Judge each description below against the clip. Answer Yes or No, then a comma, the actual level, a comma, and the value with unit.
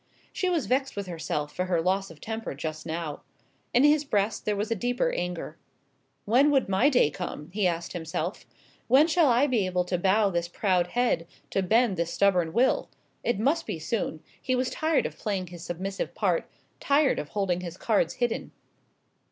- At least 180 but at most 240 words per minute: Yes, average, 190 wpm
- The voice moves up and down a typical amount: No, wide, 6.1 semitones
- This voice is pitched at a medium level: No, high, 195 Hz